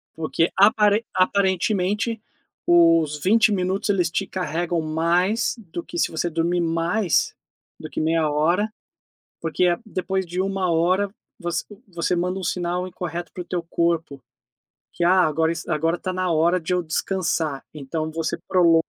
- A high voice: No, medium, 175 Hz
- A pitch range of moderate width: No, narrow, 2.3 semitones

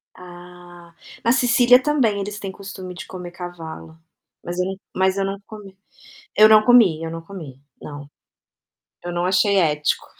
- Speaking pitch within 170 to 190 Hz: Yes, medium, 185 Hz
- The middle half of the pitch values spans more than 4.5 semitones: No, average, 2.8 semitones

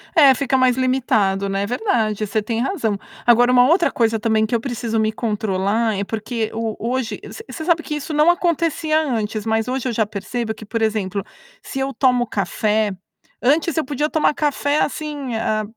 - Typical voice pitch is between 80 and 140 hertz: No, high, 235 Hz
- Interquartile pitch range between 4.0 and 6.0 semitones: Yes, average, 4.4 semitones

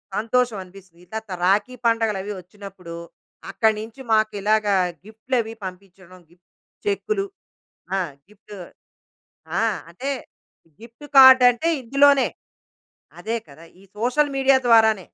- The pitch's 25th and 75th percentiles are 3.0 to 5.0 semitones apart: Yes, average, 4.2 semitones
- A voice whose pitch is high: Yes, high, 220 Hz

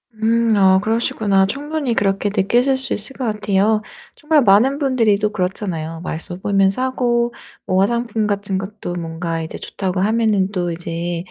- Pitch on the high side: Yes, high, 205 Hz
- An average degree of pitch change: Yes, average, 3.7 semitones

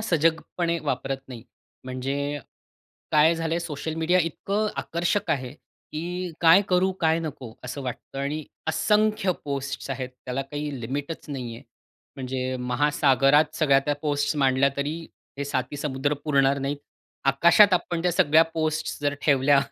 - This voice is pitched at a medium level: Yes, medium, 145 Hz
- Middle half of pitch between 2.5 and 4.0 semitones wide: Yes, average, 3.3 semitones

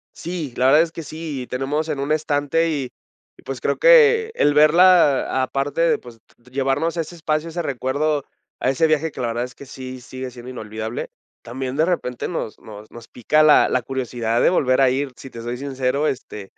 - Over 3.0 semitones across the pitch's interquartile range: Yes, average, 3.7 semitones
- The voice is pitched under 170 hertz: Yes, low, 135 Hz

